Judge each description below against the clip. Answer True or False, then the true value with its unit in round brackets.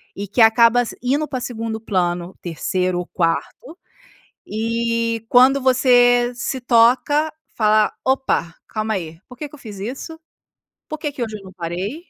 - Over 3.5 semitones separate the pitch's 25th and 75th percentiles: True (4.2 semitones)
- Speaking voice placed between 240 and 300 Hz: False (230 Hz)